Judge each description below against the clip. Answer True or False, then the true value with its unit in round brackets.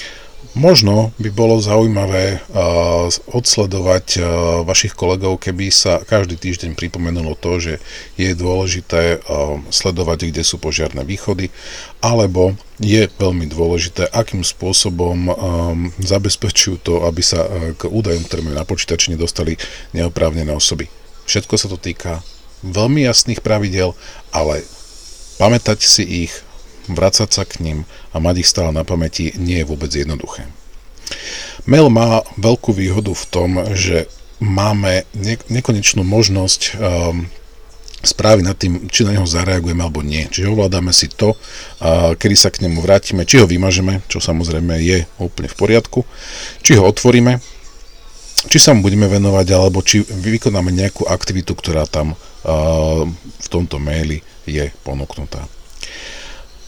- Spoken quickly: False (135 wpm)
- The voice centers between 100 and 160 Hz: False (90 Hz)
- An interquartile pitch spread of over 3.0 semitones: True (3.4 semitones)